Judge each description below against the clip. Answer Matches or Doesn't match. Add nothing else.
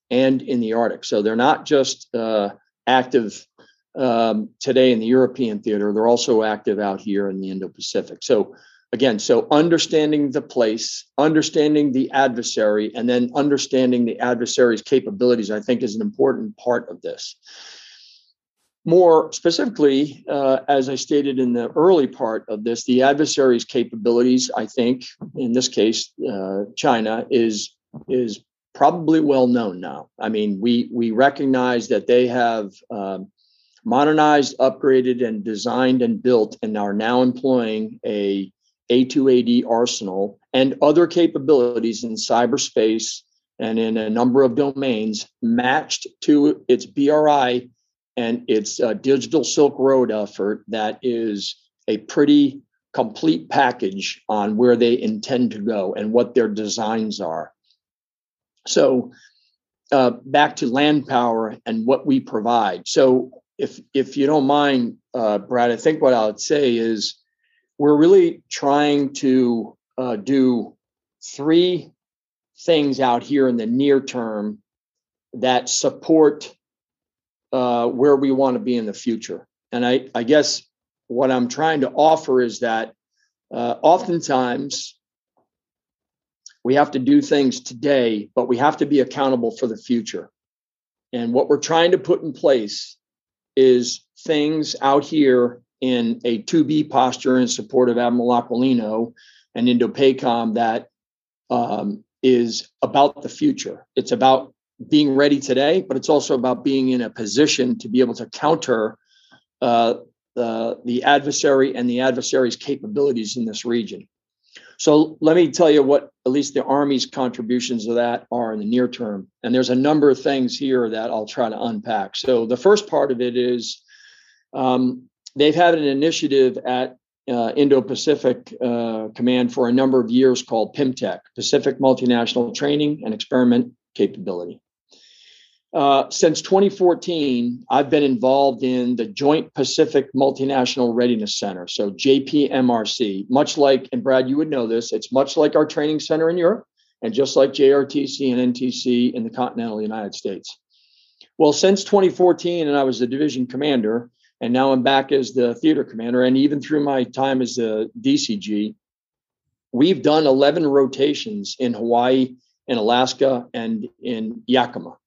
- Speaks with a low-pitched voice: Matches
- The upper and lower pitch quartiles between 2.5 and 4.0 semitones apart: Matches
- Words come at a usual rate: Matches